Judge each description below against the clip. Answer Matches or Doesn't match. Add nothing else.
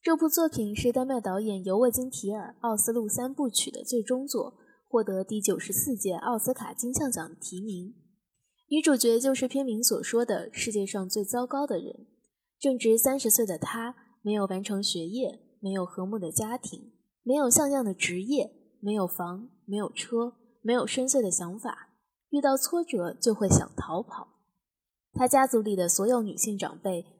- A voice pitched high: Matches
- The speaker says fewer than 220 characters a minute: Doesn't match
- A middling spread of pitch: Matches